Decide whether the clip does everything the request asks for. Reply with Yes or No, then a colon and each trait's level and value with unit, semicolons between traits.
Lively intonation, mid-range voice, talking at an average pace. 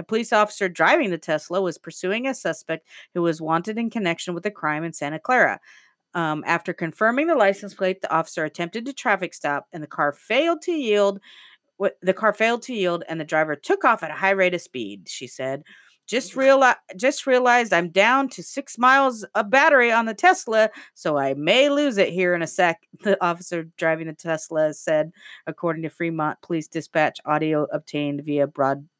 Yes: wide, 5.8 semitones; medium, 175 Hz; average, 195 wpm